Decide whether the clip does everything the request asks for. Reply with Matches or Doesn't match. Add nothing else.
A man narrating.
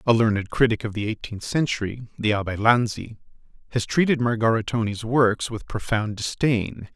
Matches